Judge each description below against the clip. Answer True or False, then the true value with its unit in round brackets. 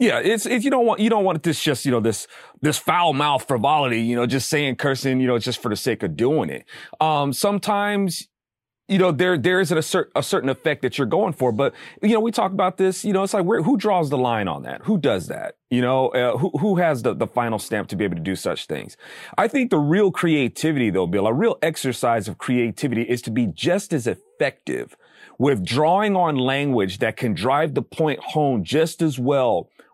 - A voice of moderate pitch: True (155 Hz)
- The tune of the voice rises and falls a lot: True (7.2 semitones)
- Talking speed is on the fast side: True (235 wpm)